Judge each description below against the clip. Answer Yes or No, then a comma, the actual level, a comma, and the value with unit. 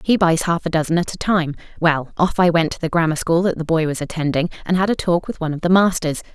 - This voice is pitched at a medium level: Yes, medium, 170 Hz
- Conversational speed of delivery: No, fast, 285 wpm